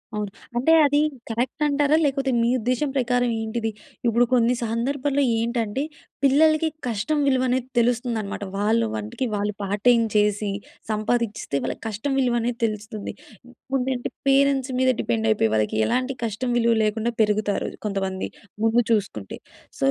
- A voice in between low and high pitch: No, high, 235 Hz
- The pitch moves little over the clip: No, average, 3.6 semitones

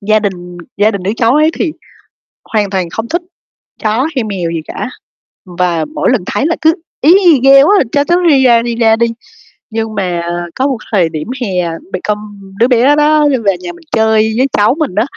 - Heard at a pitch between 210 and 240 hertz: Yes, high, 220 Hz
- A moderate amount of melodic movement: No, wide, 6.1 semitones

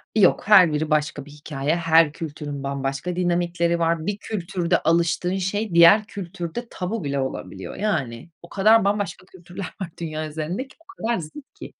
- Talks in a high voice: No, medium, 170 Hz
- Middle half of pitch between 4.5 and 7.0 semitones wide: No, average, 4.1 semitones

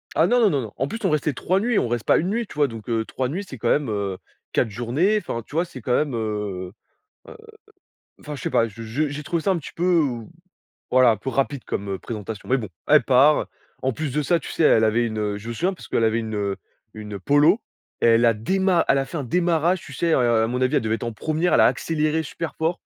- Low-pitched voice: Yes, low, 130 Hz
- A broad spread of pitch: Yes, wide, 6.3 semitones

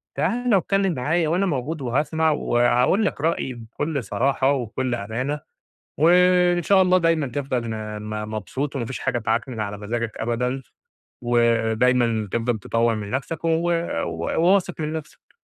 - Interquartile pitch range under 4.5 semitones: No, wide, 5.6 semitones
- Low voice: Yes, low, 130 Hz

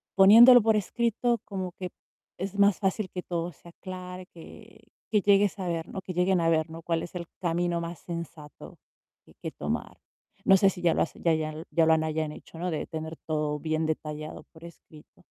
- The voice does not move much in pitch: No, average, 3.0 semitones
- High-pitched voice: No, medium, 175 Hz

